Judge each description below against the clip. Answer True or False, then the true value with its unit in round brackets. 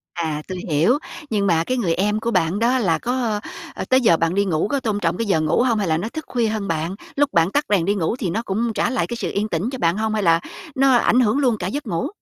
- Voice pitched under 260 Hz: True (210 Hz)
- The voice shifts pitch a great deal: True (5.8 semitones)